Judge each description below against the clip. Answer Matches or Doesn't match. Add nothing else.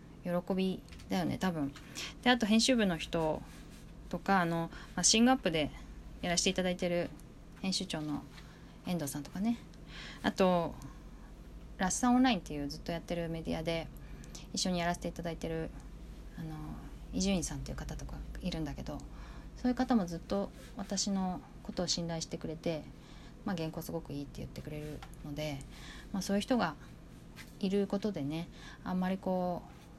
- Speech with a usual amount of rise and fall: Matches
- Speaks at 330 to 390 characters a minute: Matches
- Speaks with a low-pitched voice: Doesn't match